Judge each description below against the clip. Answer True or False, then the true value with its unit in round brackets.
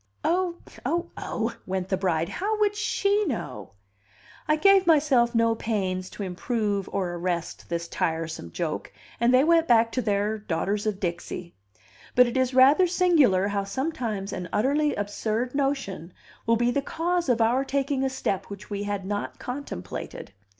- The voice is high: True (230 Hz)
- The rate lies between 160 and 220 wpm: True (165 wpm)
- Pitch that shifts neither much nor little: False (6.6 semitones)